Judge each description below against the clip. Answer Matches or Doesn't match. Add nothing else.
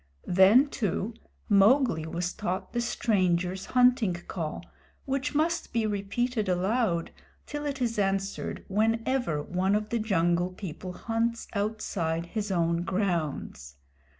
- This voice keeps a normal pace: Doesn't match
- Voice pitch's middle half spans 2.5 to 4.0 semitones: Doesn't match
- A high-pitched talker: Matches